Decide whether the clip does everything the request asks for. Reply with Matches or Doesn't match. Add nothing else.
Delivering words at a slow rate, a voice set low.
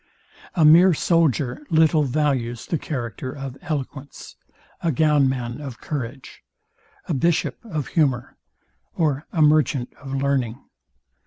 Doesn't match